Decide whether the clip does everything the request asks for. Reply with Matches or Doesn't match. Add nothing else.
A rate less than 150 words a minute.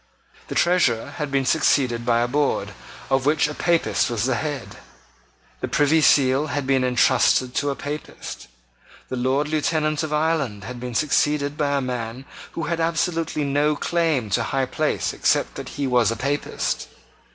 Doesn't match